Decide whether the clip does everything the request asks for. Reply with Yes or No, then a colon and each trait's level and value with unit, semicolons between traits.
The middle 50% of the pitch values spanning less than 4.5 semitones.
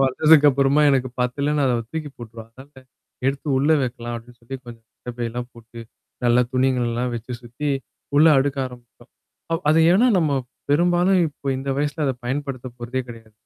Yes: average, 3.3 semitones